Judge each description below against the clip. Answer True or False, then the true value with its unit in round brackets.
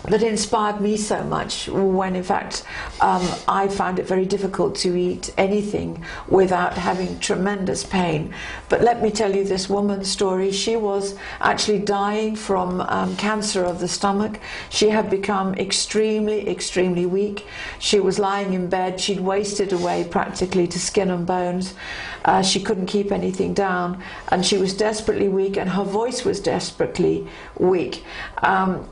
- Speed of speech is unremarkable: True (160 wpm)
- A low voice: False (195 Hz)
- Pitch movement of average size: False (1.8 semitones)